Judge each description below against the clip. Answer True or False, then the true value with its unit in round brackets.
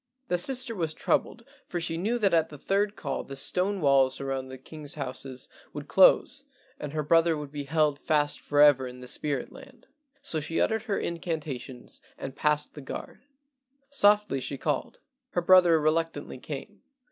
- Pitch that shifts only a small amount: False (4.4 semitones)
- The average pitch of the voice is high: False (155 Hz)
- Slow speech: False (170 wpm)